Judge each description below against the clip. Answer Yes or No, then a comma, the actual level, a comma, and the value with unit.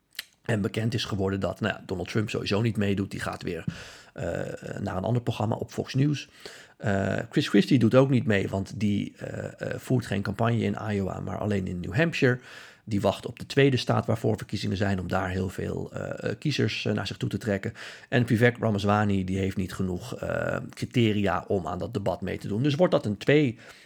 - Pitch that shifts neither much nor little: Yes, average, 3.7 semitones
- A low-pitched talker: Yes, low, 105 Hz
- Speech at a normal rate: No, fast, 215 wpm